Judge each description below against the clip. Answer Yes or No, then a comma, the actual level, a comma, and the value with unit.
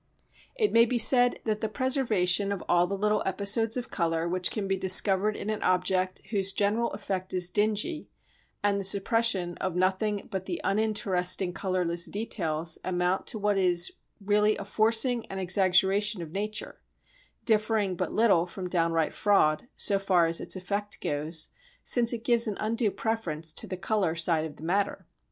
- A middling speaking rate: Yes, average, 170 wpm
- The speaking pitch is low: No, high, 195 Hz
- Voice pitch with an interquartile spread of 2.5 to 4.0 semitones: Yes, average, 3.2 semitones